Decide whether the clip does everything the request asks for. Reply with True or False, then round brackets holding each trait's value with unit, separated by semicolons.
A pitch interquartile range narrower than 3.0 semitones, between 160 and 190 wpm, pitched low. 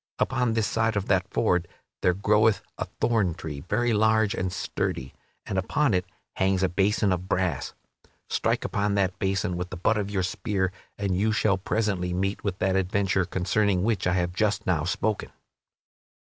True (2.6 semitones; 175 wpm; 95 Hz)